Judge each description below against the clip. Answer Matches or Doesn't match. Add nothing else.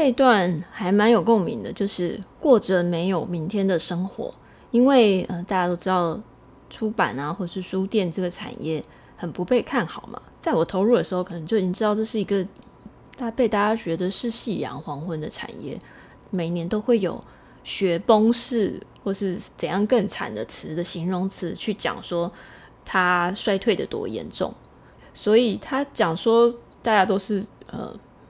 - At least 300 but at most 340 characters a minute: Doesn't match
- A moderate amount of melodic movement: Matches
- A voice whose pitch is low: Doesn't match